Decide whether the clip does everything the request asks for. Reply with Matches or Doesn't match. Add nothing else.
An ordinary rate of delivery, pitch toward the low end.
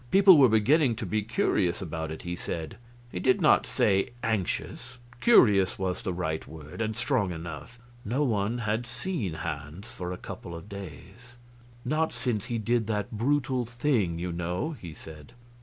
Matches